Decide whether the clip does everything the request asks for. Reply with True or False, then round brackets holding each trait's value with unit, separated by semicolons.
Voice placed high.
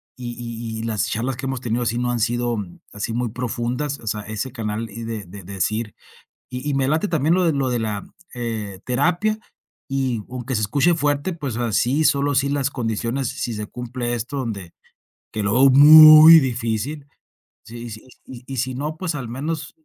False (125 Hz)